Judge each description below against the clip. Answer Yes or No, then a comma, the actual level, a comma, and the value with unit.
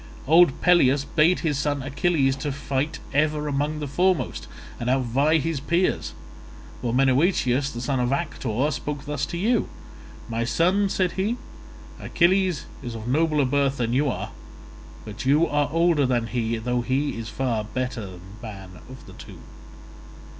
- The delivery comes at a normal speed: Yes, average, 155 wpm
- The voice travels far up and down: No, average, 4.2 semitones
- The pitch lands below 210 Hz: Yes, medium, 140 Hz